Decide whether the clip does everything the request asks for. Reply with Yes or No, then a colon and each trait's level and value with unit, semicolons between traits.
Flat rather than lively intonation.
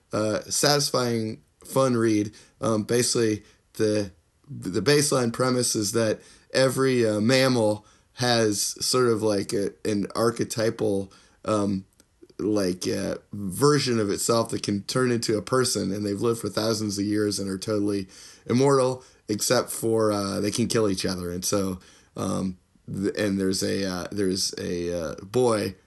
No: average, 3.2 semitones